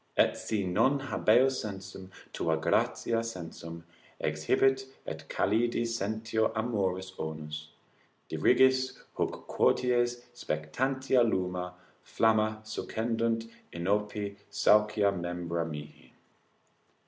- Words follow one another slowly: Yes, slow, 90 wpm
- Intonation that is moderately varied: Yes, average, 4.7 semitones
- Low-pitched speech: Yes, low, 105 Hz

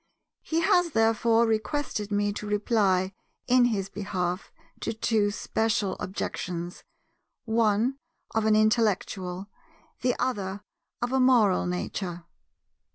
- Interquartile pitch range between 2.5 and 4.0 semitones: Yes, average, 3.1 semitones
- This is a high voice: Yes, high, 215 Hz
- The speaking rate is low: Yes, slow, 110 wpm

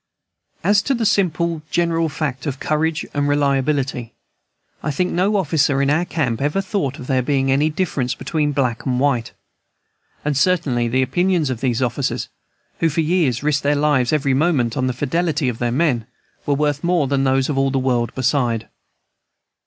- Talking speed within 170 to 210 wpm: Yes, average, 180 wpm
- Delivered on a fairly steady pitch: No, average, 3.7 semitones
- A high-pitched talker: No, medium, 145 Hz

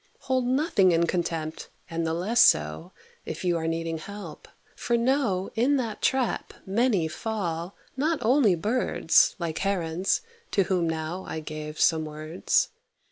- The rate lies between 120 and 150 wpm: Yes, average, 145 wpm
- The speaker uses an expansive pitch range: Yes, wide, 6.1 semitones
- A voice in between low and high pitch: Yes, medium, 180 Hz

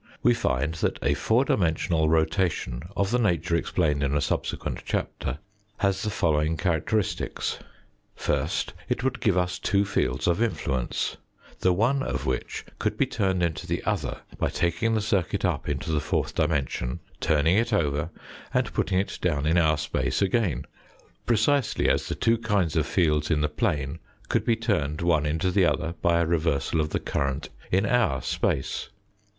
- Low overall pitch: Yes, very low, 85 Hz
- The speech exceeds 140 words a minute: Yes, average, 170 wpm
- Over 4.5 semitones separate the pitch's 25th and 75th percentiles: Yes, average, 5.0 semitones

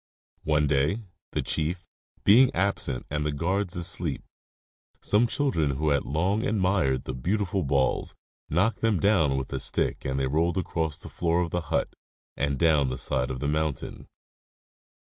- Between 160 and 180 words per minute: Yes, average, 165 wpm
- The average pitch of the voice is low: Yes, very low, 80 Hz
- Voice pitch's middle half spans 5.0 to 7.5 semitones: Yes, average, 5.3 semitones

